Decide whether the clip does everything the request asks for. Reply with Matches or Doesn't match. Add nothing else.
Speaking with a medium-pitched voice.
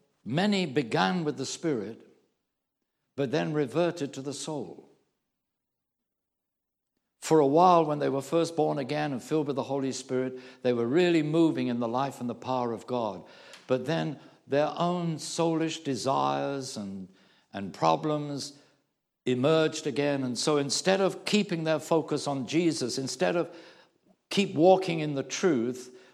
Matches